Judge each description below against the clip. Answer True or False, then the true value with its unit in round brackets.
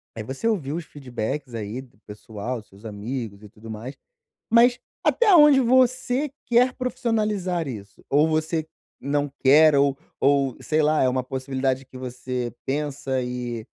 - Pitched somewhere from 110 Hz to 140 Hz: True (135 Hz)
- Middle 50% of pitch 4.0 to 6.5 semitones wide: True (4.8 semitones)